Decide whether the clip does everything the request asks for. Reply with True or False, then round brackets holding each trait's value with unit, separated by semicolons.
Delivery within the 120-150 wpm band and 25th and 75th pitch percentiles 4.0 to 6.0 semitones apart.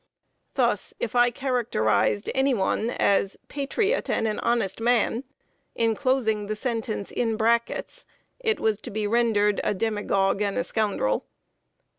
False (135 wpm; 2.9 semitones)